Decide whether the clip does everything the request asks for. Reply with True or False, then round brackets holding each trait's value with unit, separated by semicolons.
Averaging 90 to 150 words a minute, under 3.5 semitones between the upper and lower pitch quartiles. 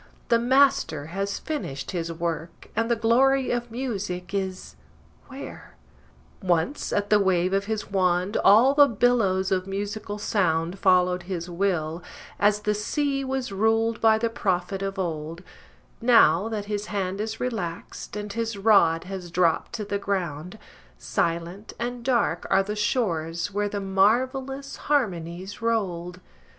False (145 wpm; 4.1 semitones)